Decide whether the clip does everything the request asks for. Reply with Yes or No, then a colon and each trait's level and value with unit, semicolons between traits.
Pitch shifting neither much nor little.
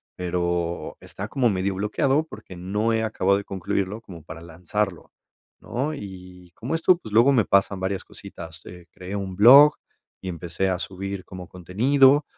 Yes: average, 3.7 semitones